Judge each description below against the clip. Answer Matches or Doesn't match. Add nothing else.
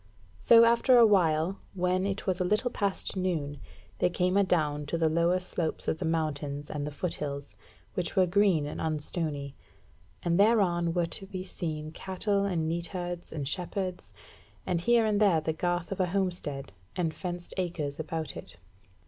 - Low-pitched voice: Doesn't match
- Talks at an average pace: Matches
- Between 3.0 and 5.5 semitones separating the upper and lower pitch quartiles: Matches